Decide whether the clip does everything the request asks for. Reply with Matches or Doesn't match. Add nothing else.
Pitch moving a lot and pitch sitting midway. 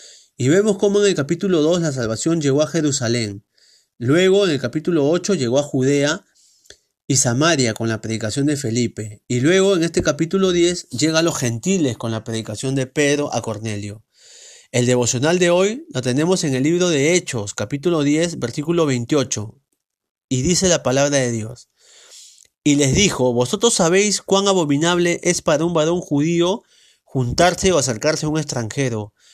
Matches